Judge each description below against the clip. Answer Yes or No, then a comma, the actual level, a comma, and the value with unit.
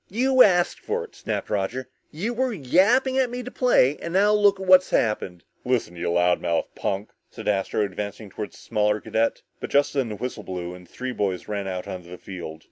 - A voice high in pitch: No, low, 115 Hz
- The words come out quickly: Yes, fast, 210 wpm